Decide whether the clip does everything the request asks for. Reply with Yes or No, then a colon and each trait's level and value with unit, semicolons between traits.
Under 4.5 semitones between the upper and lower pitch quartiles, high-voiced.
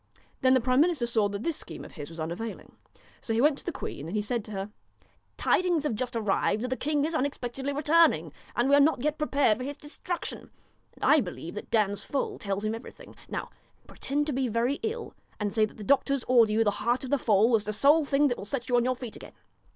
No: average, 5.0 semitones; very high, 250 Hz